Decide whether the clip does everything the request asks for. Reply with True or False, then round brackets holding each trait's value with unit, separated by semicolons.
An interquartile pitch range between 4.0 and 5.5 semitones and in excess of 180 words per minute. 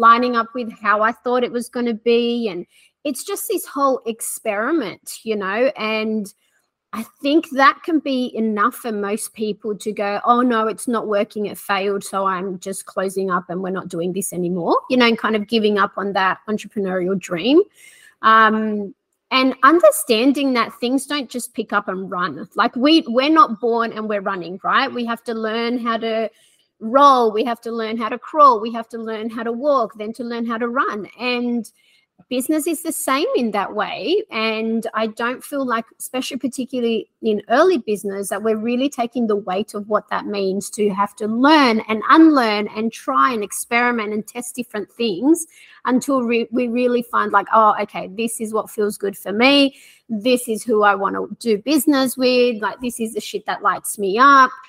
False (3.4 semitones; 200 wpm)